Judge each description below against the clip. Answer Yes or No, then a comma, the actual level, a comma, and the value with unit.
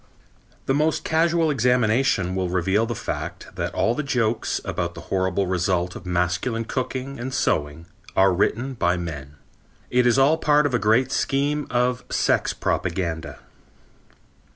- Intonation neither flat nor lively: No, wide, 6.7 semitones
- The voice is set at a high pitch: No, low, 115 Hz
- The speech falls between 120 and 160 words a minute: Yes, average, 150 wpm